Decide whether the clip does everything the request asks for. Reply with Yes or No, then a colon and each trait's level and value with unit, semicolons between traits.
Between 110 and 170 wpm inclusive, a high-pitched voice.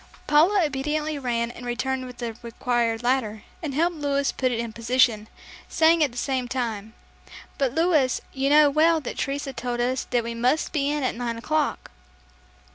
No: average, 180 wpm; very high, 260 Hz